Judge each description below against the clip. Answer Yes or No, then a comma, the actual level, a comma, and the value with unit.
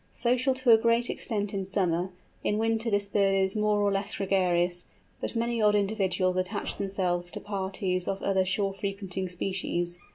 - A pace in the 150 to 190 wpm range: Yes, average, 170 wpm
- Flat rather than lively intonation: Yes, narrow, 2.3 semitones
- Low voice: No, high, 195 Hz